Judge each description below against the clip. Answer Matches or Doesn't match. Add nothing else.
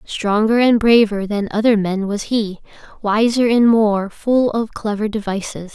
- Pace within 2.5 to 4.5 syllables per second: Matches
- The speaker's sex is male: Doesn't match